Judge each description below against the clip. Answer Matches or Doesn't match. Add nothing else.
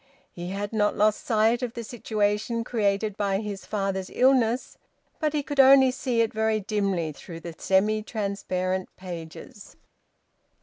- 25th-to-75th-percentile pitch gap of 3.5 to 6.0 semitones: Doesn't match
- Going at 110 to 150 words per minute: Matches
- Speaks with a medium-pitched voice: Doesn't match